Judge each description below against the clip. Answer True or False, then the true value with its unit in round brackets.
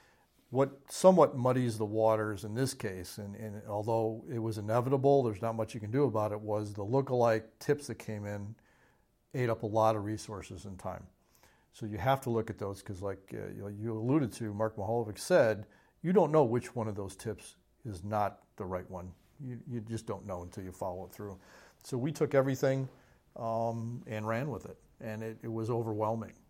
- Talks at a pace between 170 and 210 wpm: True (205 wpm)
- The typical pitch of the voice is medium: False (110 Hz)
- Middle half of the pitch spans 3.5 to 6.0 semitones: False (2.8 semitones)